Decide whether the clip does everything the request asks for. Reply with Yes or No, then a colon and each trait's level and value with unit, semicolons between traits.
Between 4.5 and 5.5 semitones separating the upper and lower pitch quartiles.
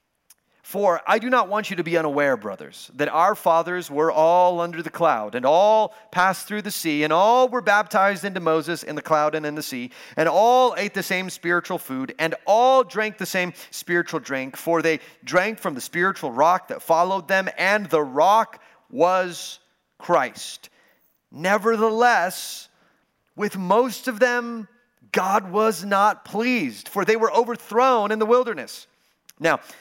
Yes: average, 4.8 semitones